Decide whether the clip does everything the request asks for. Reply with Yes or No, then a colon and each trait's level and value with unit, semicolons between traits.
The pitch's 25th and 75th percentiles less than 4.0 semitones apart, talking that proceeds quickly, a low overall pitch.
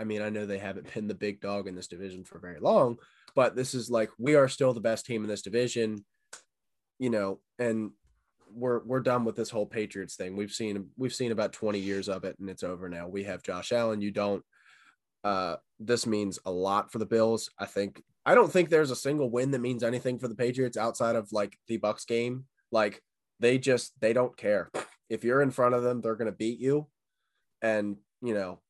Yes: average, 3.4 semitones; fast, 225 wpm; low, 110 Hz